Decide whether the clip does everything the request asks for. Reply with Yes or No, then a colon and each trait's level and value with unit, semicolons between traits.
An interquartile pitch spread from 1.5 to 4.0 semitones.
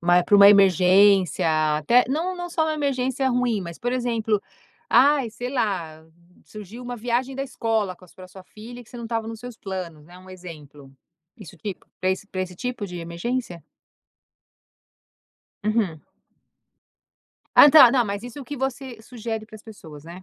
No: average, 5.2 semitones